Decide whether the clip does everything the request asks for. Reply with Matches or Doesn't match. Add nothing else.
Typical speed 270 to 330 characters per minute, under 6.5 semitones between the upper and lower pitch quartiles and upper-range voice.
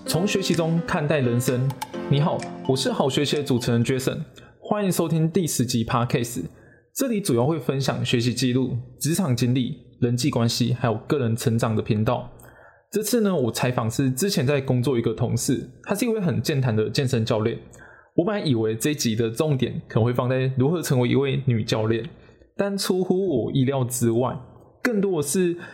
Doesn't match